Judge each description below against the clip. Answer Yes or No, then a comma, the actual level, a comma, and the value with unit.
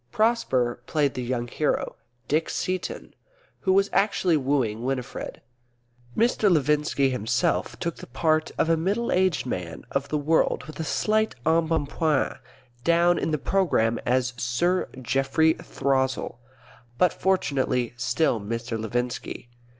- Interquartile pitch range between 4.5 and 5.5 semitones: Yes, average, 5.2 semitones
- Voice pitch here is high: No, medium, 145 Hz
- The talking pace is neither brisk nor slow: No, slow, 130 wpm